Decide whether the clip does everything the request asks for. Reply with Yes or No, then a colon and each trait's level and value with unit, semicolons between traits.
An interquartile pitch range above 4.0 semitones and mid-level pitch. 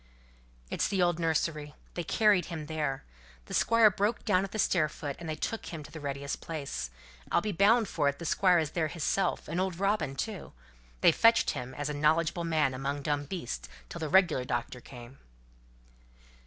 Yes: average, 4.4 semitones; medium, 160 Hz